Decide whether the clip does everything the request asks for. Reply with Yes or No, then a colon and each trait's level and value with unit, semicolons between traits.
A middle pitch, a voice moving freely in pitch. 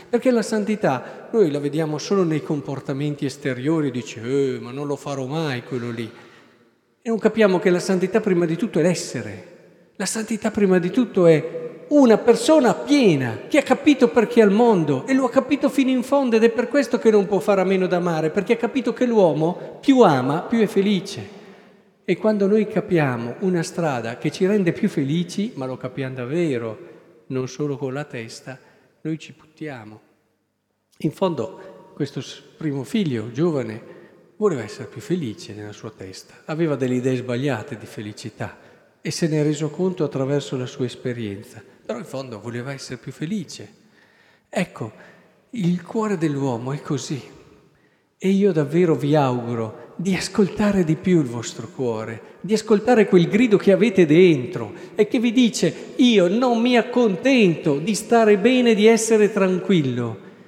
Yes: medium, 170 Hz; wide, 7.8 semitones